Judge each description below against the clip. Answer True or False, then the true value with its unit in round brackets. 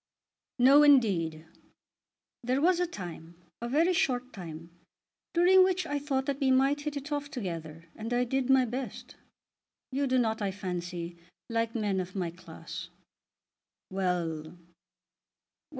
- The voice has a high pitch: True (245 Hz)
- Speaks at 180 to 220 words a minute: False (145 wpm)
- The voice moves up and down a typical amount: False (7.9 semitones)